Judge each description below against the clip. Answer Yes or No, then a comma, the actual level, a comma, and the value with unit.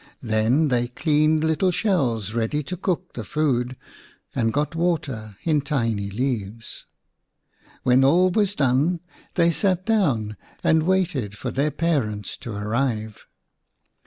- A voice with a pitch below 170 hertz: Yes, medium, 140 Hz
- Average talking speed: No, slow, 130 wpm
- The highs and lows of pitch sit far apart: Yes, wide, 6.6 semitones